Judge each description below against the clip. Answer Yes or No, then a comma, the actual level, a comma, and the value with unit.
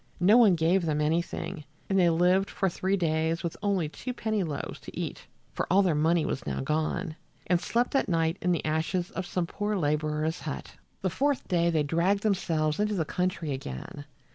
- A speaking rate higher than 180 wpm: Yes, average, 195 wpm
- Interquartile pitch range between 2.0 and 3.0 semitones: No, average, 3.5 semitones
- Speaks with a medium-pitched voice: Yes, medium, 170 Hz